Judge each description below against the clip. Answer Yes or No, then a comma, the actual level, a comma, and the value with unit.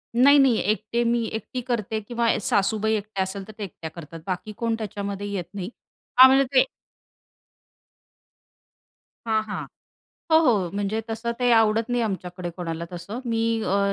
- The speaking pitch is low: No, high, 215 Hz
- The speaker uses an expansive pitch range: No, average, 3.0 semitones